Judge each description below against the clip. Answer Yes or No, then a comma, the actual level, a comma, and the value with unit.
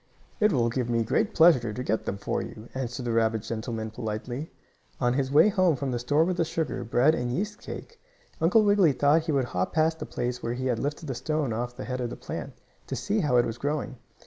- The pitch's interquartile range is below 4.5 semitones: No, average, 5.1 semitones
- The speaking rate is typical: No, fast, 240 wpm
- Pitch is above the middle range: No, low, 130 Hz